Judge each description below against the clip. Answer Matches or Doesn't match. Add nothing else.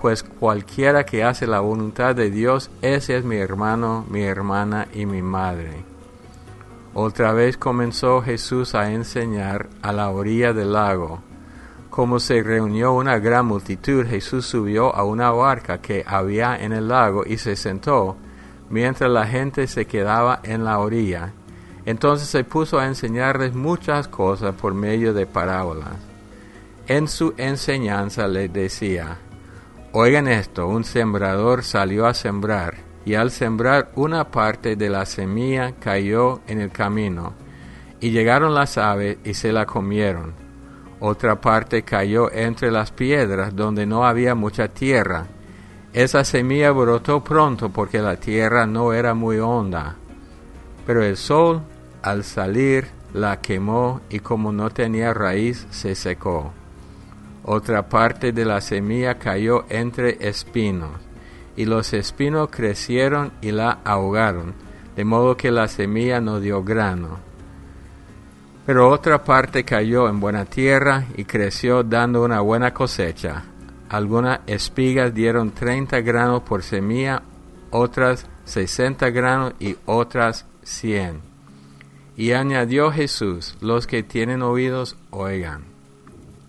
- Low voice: Matches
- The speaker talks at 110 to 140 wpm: Matches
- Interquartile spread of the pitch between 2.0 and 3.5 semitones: Doesn't match